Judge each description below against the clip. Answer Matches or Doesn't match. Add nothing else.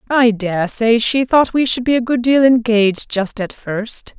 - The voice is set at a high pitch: Matches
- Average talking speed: Doesn't match